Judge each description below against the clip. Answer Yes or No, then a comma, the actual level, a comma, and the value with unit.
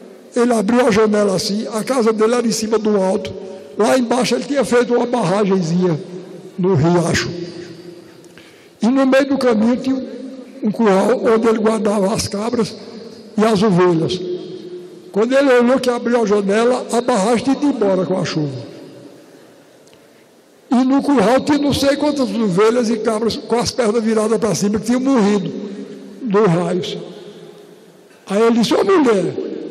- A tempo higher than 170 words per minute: No, average, 160 wpm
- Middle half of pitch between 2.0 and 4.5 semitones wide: Yes, average, 4.1 semitones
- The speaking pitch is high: Yes, high, 220 Hz